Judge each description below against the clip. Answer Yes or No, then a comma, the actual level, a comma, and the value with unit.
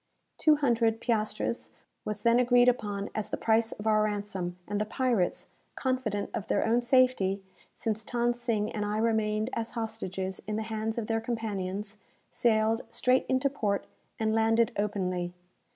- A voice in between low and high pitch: No, high, 220 Hz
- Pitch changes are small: Yes, narrow, 2.3 semitones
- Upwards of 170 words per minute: No, average, 160 wpm